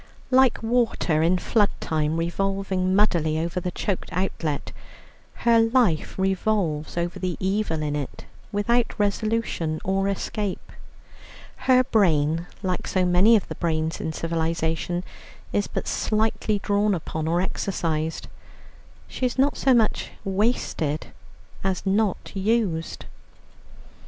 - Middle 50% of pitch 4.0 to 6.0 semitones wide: Yes, average, 4.5 semitones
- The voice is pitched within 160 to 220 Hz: Yes, high, 190 Hz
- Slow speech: Yes, slow, 120 wpm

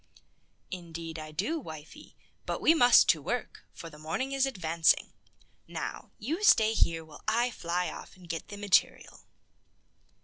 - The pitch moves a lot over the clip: Yes, wide, 6.7 semitones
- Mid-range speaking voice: Yes, medium, 180 Hz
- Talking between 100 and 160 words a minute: Yes, average, 150 wpm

